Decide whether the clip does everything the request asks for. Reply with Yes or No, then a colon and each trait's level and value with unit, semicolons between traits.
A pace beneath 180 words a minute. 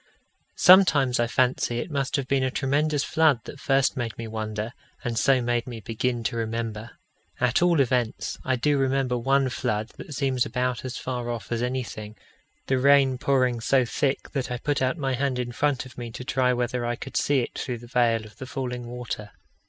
No: fast, 205 wpm